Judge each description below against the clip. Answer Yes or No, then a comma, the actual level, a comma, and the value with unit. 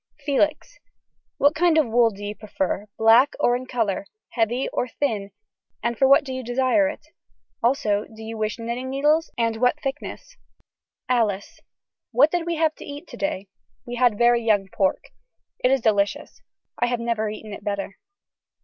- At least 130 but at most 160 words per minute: No, average, 175 wpm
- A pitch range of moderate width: Yes, average, 4.2 semitones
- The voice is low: No, high, 240 Hz